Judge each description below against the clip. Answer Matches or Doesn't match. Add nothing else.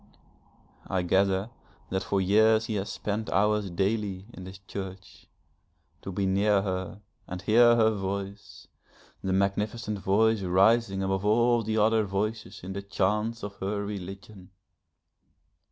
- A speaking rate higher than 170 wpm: Doesn't match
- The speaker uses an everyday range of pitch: Doesn't match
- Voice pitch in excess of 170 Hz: Doesn't match